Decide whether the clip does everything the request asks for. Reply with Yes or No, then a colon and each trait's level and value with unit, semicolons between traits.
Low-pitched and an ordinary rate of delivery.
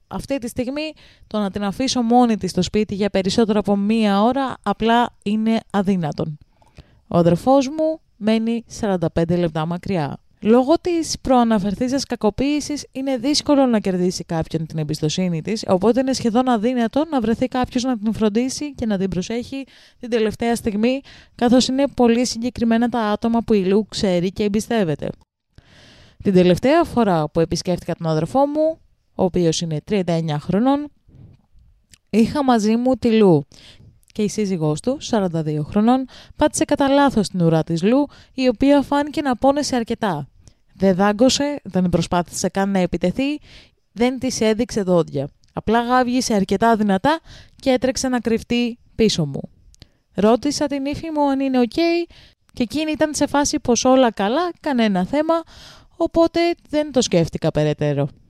No: high, 230 Hz; average, 155 wpm